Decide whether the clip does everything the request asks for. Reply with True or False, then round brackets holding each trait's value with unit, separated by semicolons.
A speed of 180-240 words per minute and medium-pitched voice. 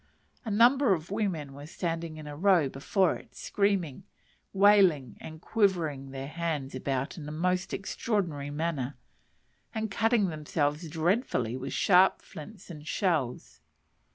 False (135 wpm; 165 Hz)